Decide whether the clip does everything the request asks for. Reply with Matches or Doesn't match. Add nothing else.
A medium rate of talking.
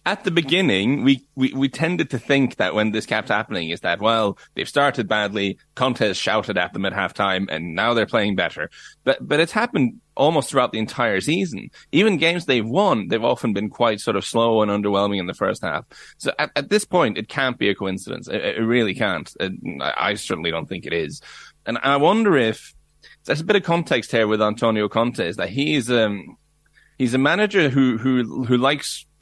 Doesn't match